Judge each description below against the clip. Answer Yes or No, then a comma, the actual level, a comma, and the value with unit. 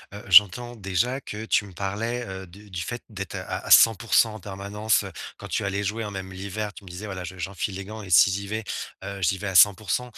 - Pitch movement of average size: No, narrow, 2.2 semitones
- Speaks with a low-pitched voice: Yes, low, 100 Hz